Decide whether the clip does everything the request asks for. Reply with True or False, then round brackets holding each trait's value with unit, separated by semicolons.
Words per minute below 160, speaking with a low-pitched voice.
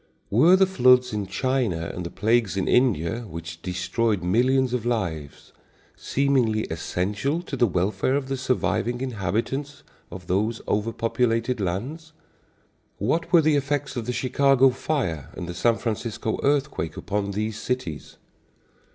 True (140 wpm; 115 Hz)